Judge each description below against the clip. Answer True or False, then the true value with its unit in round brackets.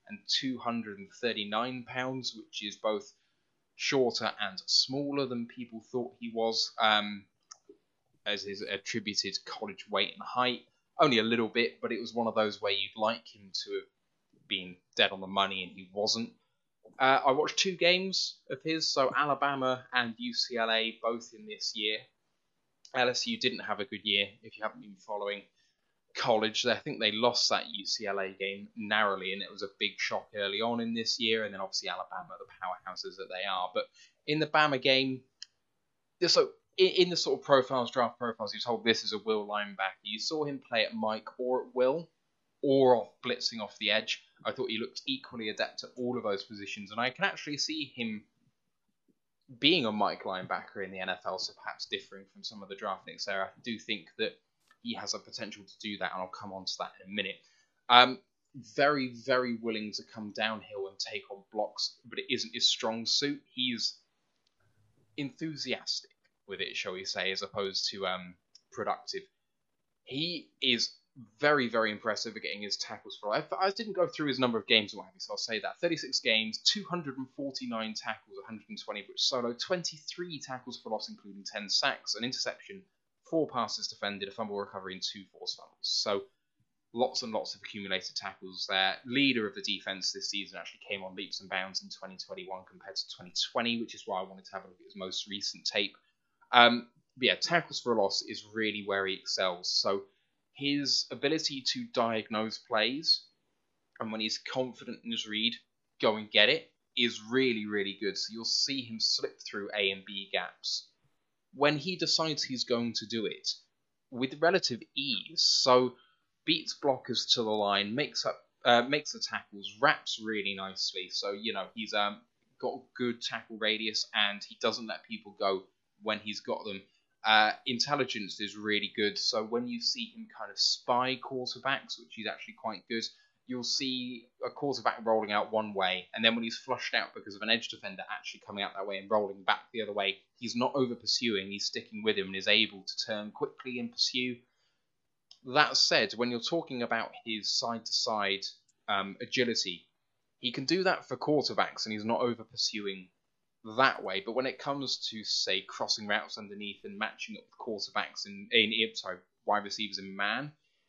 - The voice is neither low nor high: False (115 Hz)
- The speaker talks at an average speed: True (190 wpm)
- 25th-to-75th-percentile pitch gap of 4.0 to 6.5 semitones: True (4.4 semitones)